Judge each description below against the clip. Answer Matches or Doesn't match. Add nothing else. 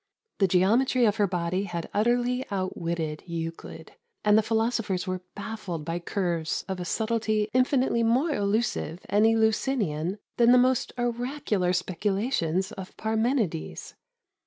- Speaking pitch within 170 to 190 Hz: Doesn't match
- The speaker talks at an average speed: Doesn't match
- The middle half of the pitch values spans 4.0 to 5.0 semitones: Matches